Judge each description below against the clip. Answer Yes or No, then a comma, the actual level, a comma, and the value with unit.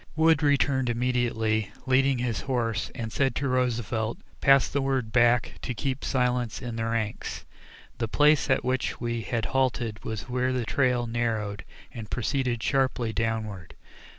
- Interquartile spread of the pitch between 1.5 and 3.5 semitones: Yes, narrow, 2.6 semitones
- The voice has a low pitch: Yes, low, 120 Hz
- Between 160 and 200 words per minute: No, average, 150 wpm